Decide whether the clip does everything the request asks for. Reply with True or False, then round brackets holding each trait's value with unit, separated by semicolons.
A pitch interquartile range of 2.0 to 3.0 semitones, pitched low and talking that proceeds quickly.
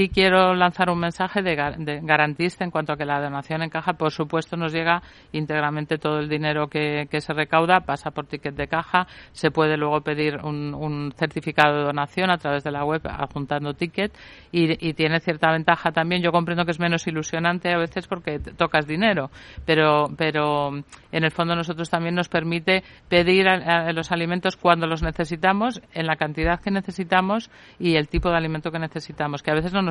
False (2.5 semitones; 165 Hz; 200 wpm)